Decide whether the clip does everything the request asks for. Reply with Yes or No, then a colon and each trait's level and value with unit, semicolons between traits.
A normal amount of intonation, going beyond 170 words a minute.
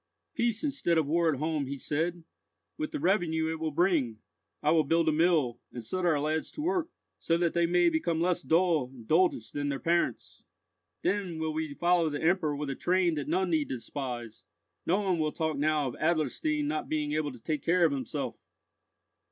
Yes: average, 3.0 semitones; average, 200 wpm